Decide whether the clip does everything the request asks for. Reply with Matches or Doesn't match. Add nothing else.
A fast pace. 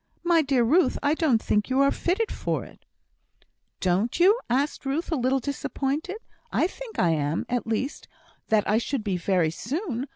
Doesn't match